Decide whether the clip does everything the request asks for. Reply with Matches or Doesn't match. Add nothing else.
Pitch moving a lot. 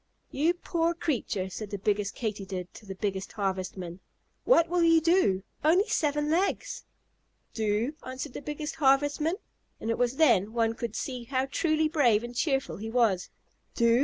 Matches